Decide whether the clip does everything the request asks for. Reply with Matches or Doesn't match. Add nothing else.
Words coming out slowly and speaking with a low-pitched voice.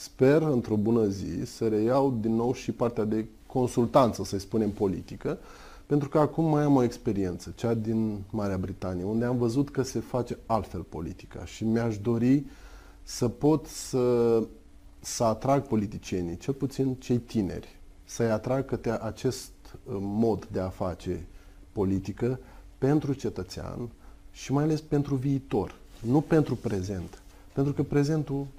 Doesn't match